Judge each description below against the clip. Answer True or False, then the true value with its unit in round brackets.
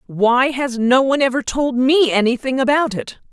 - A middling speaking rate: True (180 wpm)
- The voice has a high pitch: True (255 Hz)